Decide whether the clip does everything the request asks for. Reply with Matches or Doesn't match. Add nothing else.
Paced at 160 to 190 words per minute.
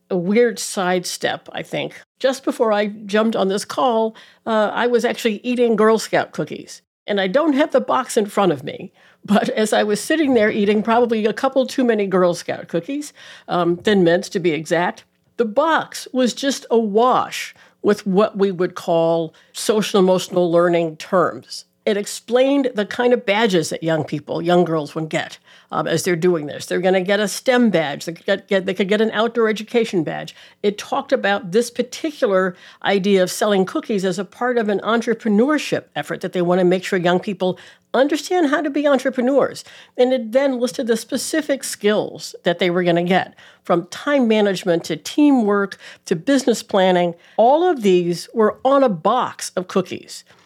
Matches